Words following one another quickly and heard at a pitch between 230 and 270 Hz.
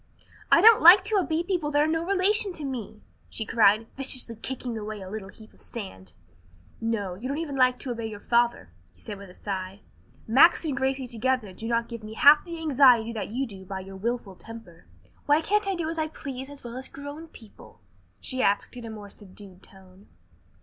Yes: fast, 210 wpm; high, 240 Hz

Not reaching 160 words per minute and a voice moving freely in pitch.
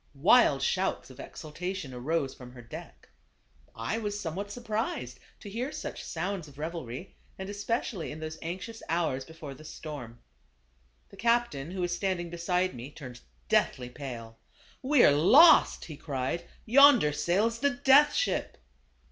Yes: average, 150 wpm; wide, 6.8 semitones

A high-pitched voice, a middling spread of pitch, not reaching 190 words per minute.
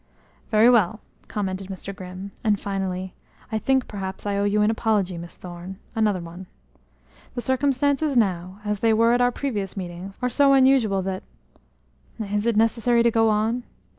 Yes: high, 210 Hz; average, 3.6 semitones; average, 165 wpm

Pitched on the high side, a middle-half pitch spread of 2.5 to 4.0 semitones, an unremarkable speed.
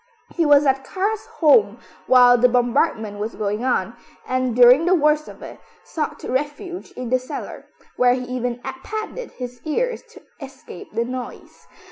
Yes: very high, 255 Hz; average, 3.6 semitones; average, 160 wpm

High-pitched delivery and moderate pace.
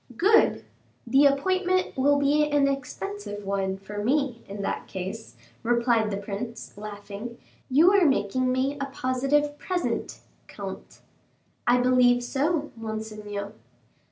No: high, 245 Hz; slow, 125 wpm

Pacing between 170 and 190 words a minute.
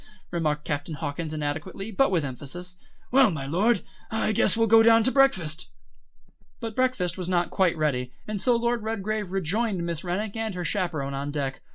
Yes: average, 180 wpm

